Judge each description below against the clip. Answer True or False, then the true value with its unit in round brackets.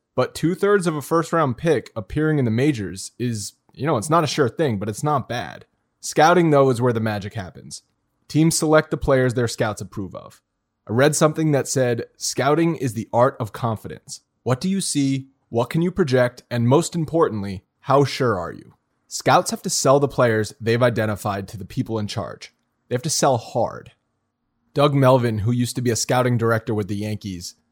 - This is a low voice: True (125 Hz)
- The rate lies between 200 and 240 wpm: True (205 wpm)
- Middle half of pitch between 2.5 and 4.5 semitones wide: False (5.0 semitones)